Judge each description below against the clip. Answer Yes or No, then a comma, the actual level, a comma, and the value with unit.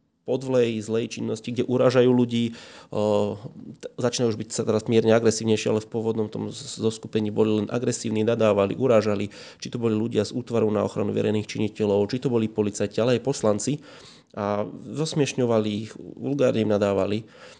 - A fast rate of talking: No, average, 155 wpm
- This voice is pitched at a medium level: No, low, 110 Hz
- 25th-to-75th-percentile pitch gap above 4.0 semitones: No, narrow, 2.5 semitones